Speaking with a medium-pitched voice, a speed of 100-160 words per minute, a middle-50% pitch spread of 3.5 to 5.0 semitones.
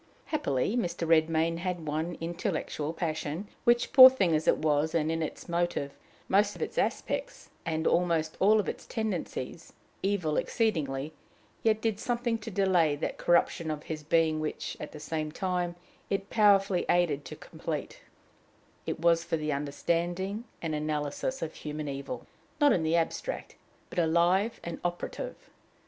Yes: medium, 170 Hz; average, 155 wpm; average, 4.0 semitones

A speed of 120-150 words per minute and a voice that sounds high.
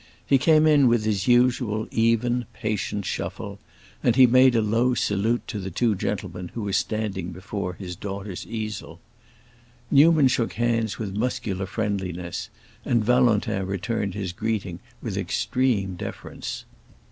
No: average, 145 wpm; low, 110 Hz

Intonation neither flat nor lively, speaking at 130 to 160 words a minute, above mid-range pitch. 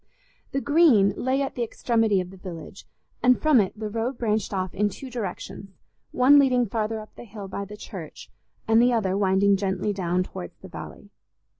No: average, 4.0 semitones; average, 190 wpm; high, 210 Hz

